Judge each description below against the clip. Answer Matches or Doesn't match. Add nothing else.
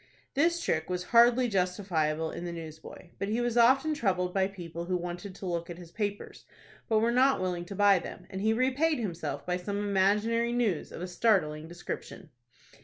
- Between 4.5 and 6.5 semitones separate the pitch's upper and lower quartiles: Matches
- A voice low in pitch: Doesn't match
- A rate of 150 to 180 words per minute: Doesn't match